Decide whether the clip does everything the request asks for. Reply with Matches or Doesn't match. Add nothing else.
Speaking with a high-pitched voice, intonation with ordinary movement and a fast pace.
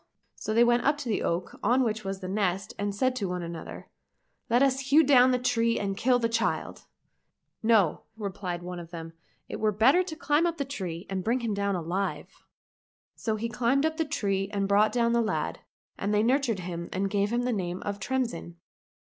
Matches